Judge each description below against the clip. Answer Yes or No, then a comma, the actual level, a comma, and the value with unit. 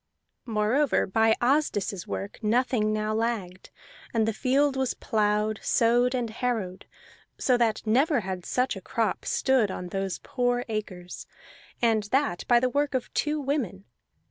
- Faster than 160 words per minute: No, average, 145 wpm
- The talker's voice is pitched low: No, high, 225 Hz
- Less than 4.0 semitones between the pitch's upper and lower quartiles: Yes, average, 3.3 semitones